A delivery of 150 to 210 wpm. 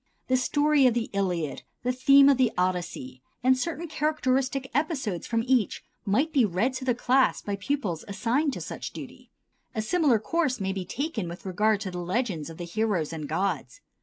Yes: average, 190 wpm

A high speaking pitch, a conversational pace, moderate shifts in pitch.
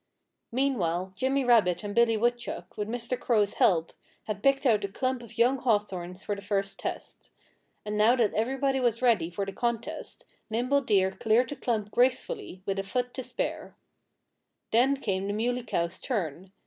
Yes: high, 225 Hz; average, 175 wpm; average, 4.0 semitones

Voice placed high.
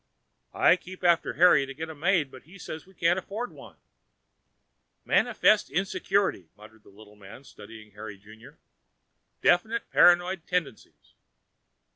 No: medium, 165 Hz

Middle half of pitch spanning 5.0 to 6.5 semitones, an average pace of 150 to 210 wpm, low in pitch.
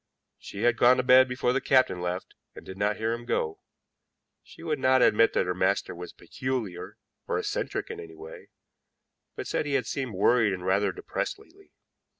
Yes: wide, 5.5 semitones; average, 190 wpm; low, 110 Hz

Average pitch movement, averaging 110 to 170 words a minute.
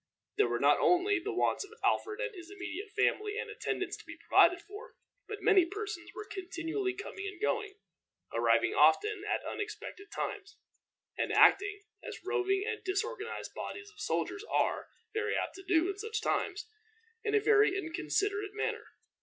No: narrow, 1.9 semitones; average, 165 wpm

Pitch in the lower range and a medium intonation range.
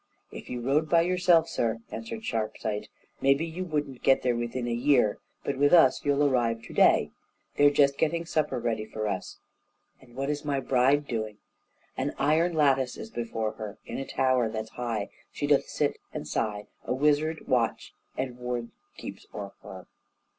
Yes: low, 130 Hz; average, 4.2 semitones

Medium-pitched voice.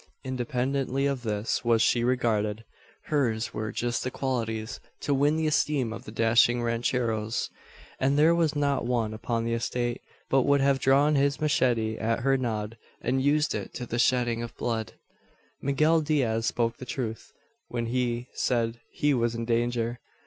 No: low, 120 Hz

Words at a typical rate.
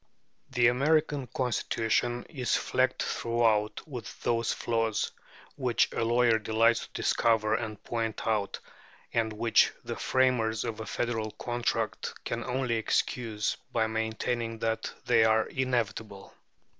No: slow, 125 wpm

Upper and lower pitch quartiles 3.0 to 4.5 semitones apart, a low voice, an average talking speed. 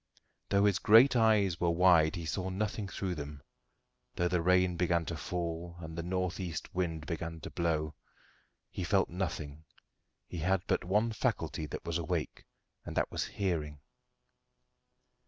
No: narrow, 2.5 semitones; very low, 85 Hz; average, 155 wpm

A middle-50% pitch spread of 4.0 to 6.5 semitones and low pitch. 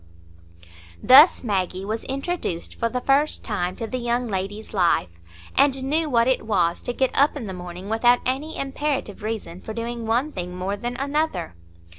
No: wide, 5.6 semitones; high, 230 Hz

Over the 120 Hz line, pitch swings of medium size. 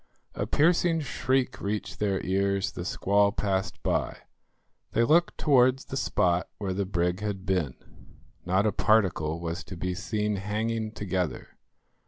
No: low, 100 Hz; average, 3.3 semitones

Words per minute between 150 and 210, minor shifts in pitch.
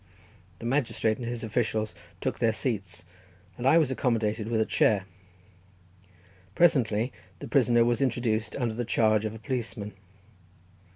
No: average, 140 wpm; narrow, 2.0 semitones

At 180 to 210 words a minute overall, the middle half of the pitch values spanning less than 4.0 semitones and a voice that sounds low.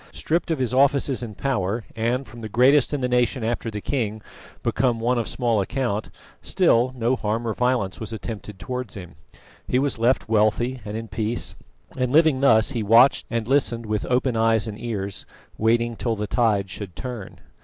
Yes: average, 185 wpm; average, 2.8 semitones; low, 115 Hz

